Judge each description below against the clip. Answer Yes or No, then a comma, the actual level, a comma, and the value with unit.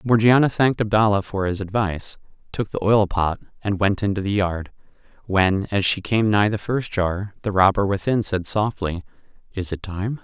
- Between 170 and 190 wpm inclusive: Yes, average, 180 wpm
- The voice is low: Yes, low, 100 Hz